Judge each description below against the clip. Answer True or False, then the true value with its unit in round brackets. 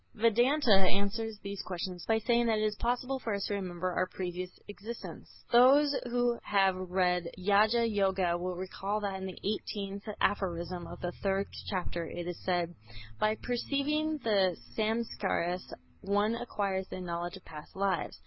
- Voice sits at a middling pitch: False (200 Hz)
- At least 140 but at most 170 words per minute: True (160 wpm)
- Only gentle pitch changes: False (3.6 semitones)